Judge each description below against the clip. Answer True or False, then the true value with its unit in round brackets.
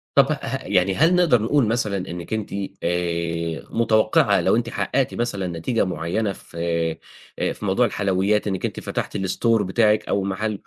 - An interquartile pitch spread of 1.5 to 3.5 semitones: False (4.1 semitones)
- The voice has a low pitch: True (105 Hz)